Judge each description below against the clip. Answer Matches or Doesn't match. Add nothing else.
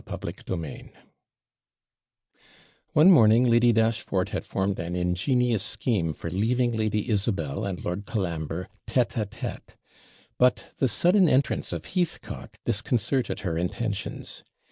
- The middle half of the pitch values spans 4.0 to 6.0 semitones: Matches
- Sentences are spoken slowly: Matches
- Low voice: Matches